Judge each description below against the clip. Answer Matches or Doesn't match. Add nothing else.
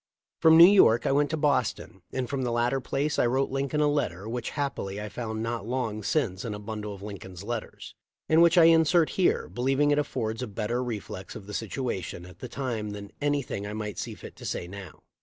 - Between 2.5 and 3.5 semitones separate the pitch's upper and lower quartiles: Doesn't match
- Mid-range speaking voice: Doesn't match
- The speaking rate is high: Matches